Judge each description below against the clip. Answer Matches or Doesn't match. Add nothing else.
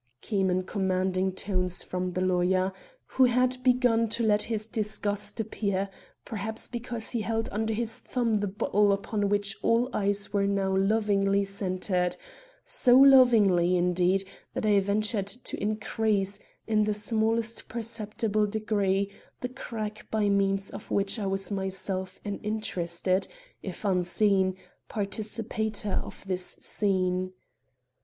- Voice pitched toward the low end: Doesn't match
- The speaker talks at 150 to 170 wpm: Doesn't match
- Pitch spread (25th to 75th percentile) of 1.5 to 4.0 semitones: Matches